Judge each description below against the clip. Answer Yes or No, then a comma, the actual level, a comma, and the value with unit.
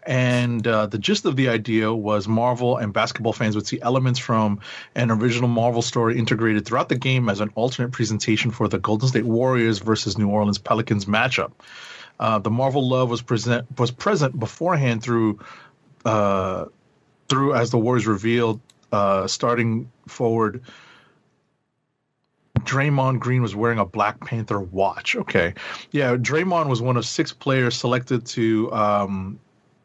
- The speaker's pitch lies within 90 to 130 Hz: Yes, low, 115 Hz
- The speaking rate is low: No, average, 155 wpm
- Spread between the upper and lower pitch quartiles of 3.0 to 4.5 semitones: No, narrow, 2.5 semitones